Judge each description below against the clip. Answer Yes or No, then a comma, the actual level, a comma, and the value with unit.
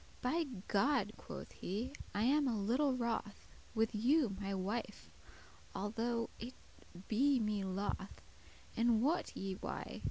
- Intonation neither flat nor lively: Yes, average, 4.0 semitones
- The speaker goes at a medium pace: No, slow, 130 wpm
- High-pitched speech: Yes, high, 230 Hz